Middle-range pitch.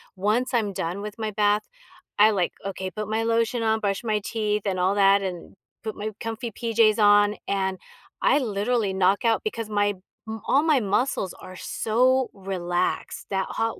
No: high, 210 Hz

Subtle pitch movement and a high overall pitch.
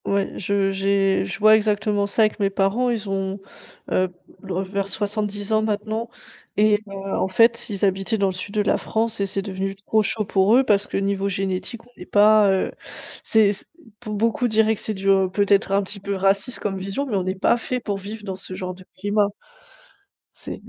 Yes: narrow, 1.8 semitones; high, 200 Hz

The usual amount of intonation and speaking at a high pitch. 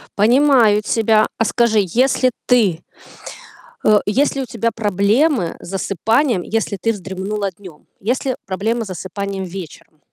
Yes: average, 3.5 semitones; high, 210 Hz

